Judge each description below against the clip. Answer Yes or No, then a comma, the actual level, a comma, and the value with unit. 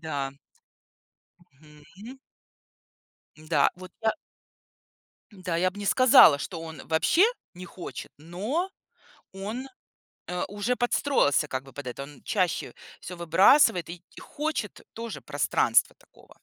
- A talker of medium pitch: Yes, medium, 180 Hz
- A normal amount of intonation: No, wide, 5.9 semitones